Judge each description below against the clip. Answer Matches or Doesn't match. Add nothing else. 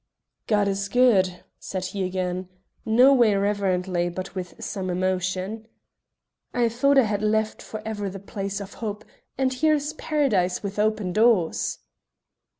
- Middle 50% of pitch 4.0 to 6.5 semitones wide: Doesn't match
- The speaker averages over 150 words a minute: Doesn't match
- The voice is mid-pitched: Doesn't match